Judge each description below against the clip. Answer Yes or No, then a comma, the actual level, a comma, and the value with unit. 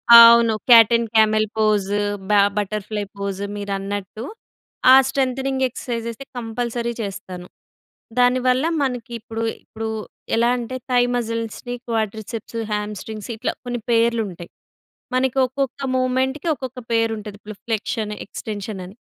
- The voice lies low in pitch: No, high, 230 Hz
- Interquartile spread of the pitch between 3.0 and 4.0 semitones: No, narrow, 2.6 semitones